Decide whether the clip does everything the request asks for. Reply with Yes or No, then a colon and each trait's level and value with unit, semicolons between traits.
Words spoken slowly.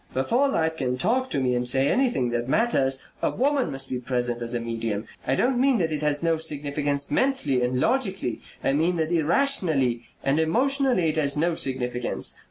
No: average, 190 wpm